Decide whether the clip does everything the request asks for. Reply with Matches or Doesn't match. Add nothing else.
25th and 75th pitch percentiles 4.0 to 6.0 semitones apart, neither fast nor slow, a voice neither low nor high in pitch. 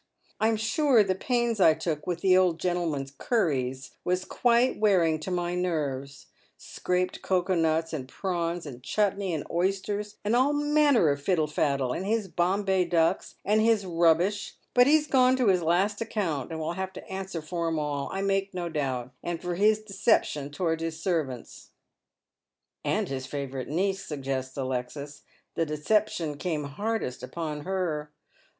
Matches